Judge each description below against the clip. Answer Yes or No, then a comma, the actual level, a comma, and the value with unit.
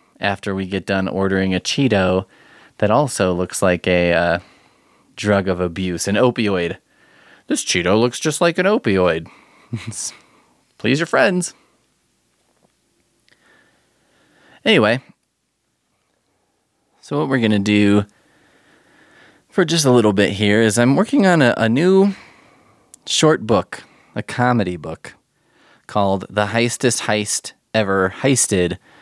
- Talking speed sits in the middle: No, slow, 120 wpm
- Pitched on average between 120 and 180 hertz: No, low, 105 Hz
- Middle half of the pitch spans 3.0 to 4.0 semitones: No, average, 4.6 semitones